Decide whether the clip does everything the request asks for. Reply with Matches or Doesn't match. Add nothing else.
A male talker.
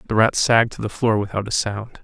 Matches